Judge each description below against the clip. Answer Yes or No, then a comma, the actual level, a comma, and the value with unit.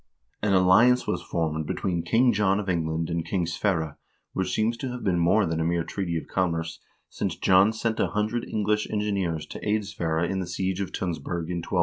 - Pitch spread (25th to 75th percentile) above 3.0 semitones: Yes, average, 3.9 semitones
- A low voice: Yes, very low, 95 Hz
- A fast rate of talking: Yes, fast, 215 wpm